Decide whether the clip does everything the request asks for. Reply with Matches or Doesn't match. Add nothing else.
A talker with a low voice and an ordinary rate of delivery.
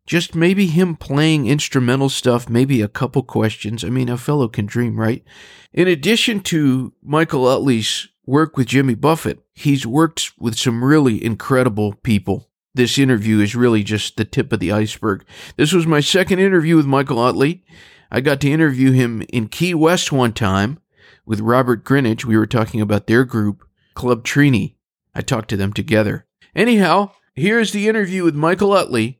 Matches